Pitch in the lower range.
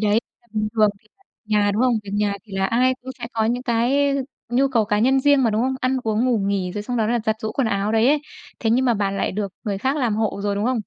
No: high, 225 Hz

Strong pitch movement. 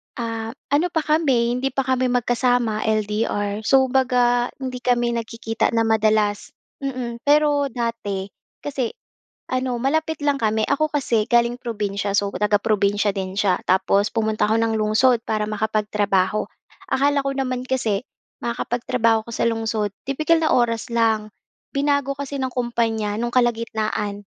No: average, 3.3 semitones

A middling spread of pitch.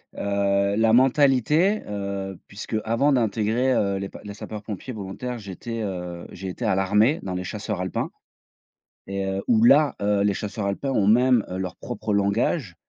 Yes: average, 3.6 semitones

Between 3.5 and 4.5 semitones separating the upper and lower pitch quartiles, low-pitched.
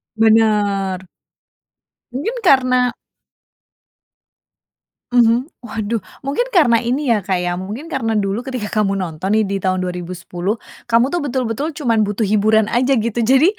No: average, 4.2 semitones; high, 225 Hz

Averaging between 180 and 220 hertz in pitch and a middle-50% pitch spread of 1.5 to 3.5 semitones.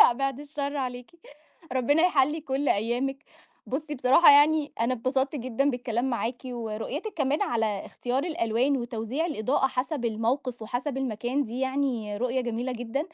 No: very high, 255 Hz; average, 3.1 semitones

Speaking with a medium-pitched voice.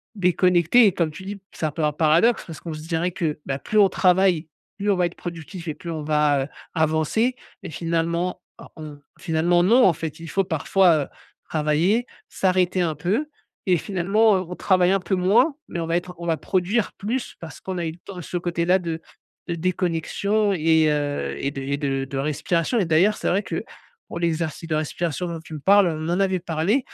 Yes: medium, 170 Hz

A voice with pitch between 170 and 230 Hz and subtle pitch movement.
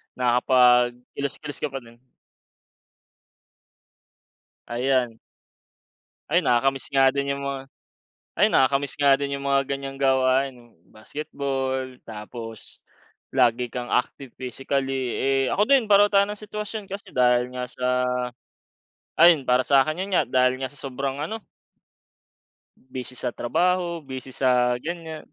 No: low, 135 Hz; narrow, 2.2 semitones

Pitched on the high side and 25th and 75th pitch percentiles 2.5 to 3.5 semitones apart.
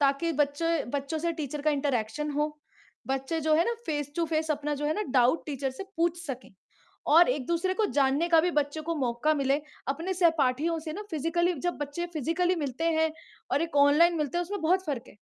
Yes: very high, 310 Hz; average, 3.1 semitones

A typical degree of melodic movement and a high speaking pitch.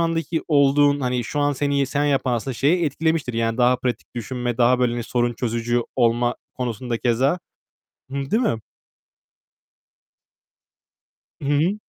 No: average, 3.2 semitones; low, 130 Hz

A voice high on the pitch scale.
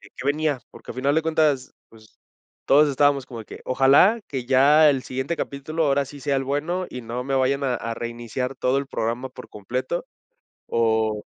No: low, 135 Hz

